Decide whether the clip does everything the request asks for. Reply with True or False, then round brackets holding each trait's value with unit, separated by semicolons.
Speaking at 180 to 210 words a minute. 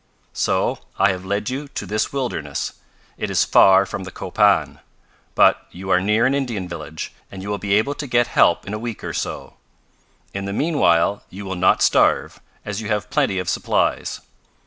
True (190 wpm)